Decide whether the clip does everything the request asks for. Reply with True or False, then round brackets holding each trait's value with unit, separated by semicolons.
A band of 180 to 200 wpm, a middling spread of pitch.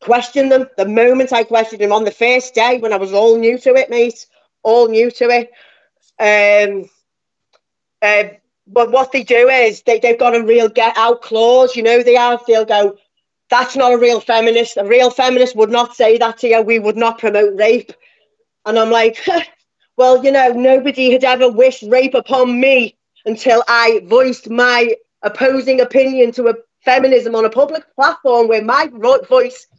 False (185 wpm; 2.2 semitones)